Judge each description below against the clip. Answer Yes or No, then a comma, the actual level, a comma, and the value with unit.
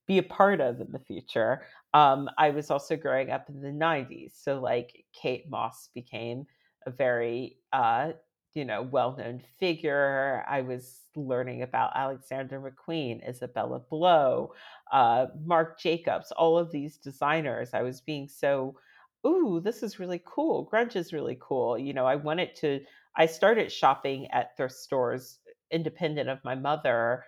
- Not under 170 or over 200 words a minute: No, average, 155 wpm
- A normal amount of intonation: Yes, average, 3.9 semitones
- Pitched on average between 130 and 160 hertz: Yes, medium, 140 Hz